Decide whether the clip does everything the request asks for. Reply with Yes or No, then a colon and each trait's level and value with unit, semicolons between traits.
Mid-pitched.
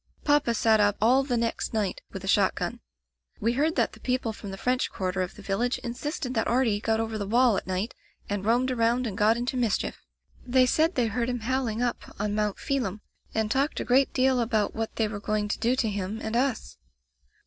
No: high, 230 Hz